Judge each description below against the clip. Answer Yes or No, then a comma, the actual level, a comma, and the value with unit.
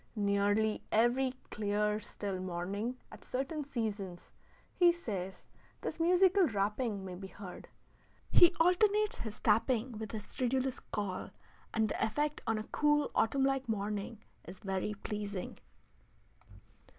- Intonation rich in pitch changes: No, average, 4.9 semitones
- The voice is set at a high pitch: Yes, high, 220 Hz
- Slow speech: Yes, slow, 125 wpm